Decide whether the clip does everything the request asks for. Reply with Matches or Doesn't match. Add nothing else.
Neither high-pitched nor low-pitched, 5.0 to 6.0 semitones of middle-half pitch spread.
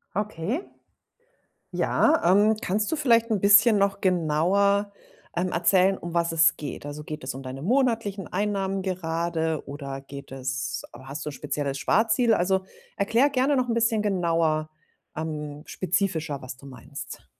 Matches